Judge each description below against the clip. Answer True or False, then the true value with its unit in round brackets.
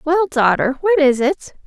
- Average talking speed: True (180 wpm)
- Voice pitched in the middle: False (300 Hz)